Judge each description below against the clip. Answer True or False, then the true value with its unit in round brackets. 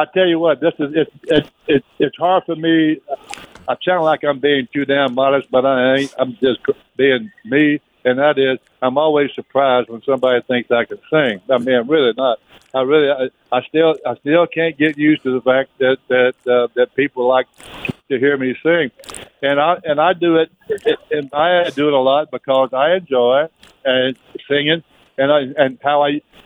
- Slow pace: False (195 wpm)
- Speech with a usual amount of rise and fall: True (3.3 semitones)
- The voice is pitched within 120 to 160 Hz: True (140 Hz)